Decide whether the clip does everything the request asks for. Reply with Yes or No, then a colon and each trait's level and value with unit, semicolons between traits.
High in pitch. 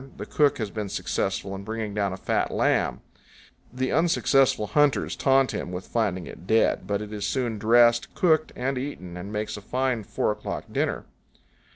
No: low, 110 Hz